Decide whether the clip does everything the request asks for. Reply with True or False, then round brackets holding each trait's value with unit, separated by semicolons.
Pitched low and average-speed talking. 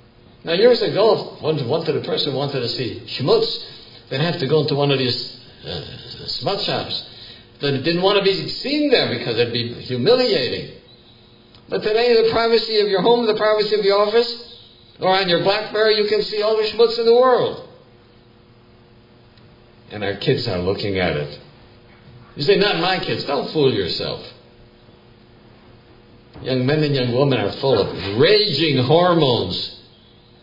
True (130 Hz; 165 wpm)